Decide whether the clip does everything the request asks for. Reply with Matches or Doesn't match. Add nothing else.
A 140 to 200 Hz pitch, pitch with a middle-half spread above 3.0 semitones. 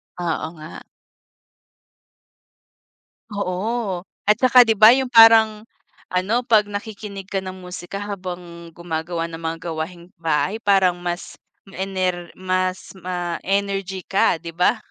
Doesn't match